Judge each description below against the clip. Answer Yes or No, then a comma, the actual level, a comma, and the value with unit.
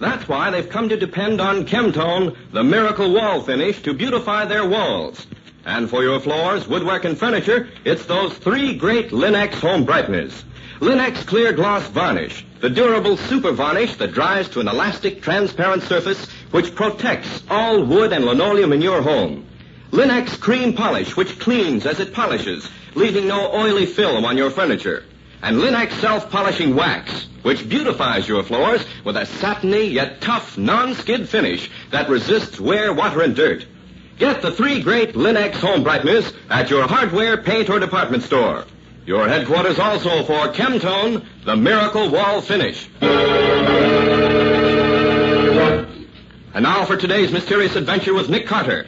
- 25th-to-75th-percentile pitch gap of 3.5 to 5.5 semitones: No, average, 2.9 semitones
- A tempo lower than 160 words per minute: Yes, average, 150 wpm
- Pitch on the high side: Yes, high, 205 Hz